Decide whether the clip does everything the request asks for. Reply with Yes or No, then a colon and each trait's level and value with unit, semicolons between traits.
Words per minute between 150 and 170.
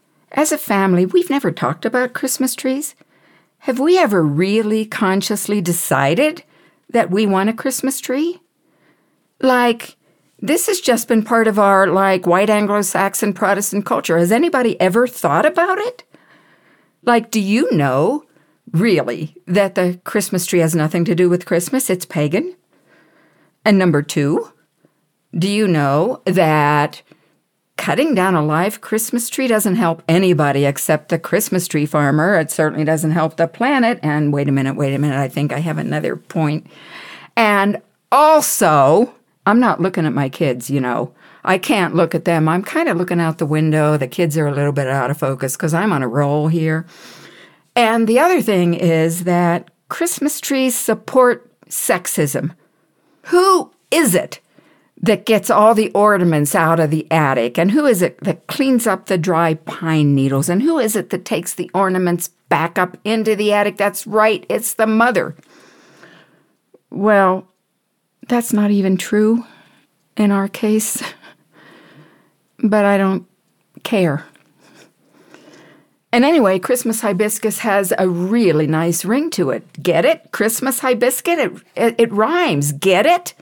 Yes: average, 155 wpm